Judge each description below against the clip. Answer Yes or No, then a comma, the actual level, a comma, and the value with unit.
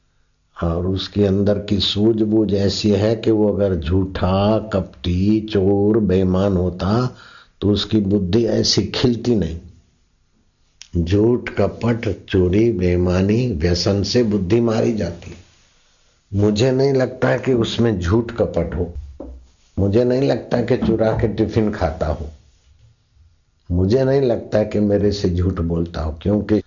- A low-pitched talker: Yes, low, 100 Hz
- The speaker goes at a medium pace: Yes, average, 135 wpm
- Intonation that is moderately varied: Yes, average, 3.8 semitones